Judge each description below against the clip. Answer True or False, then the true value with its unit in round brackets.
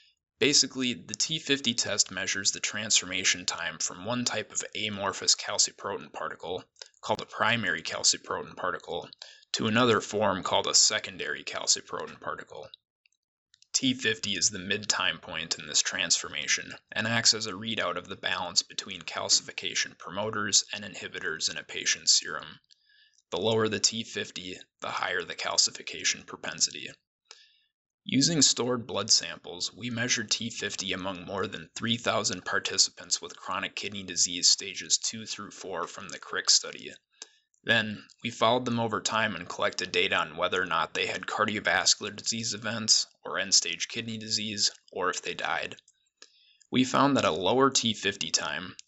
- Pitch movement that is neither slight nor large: True (3.5 semitones)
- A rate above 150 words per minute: False (145 wpm)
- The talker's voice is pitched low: True (115 Hz)